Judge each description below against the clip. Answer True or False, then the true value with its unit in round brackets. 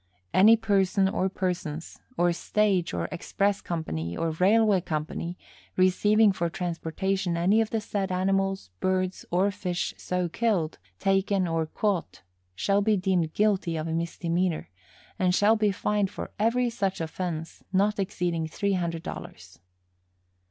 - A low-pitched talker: False (185 Hz)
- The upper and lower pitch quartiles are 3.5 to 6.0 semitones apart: False (3.1 semitones)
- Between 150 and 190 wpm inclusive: False (140 wpm)